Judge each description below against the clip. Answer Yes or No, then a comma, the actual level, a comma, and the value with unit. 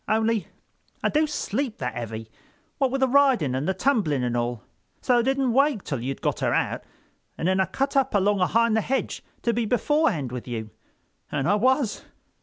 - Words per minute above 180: Yes, average, 200 wpm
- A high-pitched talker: Yes, high, 215 Hz